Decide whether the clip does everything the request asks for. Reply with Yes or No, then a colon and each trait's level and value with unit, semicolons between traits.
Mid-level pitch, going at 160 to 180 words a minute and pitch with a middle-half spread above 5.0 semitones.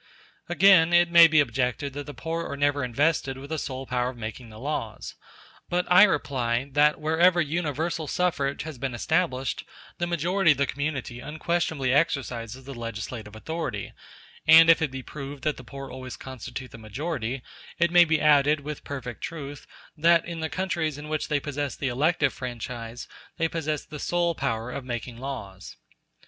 No: medium, 145 Hz; average, 175 wpm; average, 4.2 semitones